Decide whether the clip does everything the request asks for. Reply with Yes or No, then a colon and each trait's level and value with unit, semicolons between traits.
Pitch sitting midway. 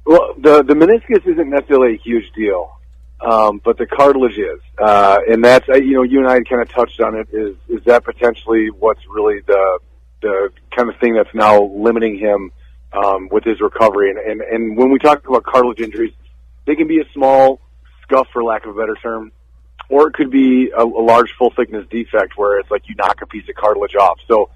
No: low, 115 Hz